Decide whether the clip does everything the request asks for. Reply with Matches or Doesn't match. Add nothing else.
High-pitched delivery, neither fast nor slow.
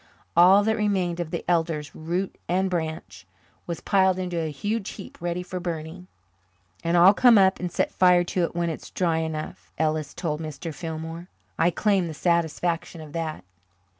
Doesn't match